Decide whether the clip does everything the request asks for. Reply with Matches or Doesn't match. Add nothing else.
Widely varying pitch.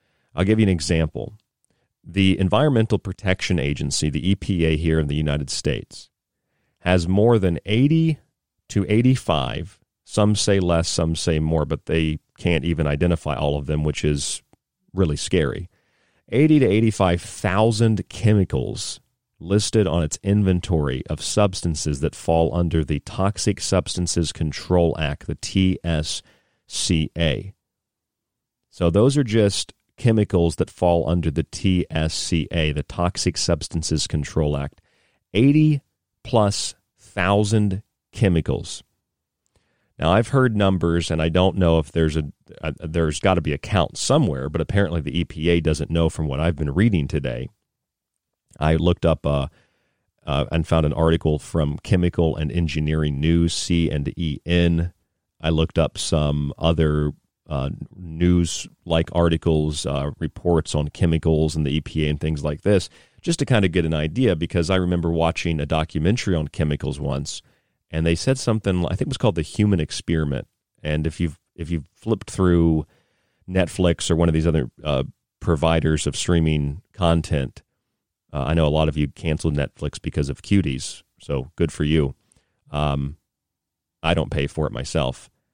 Doesn't match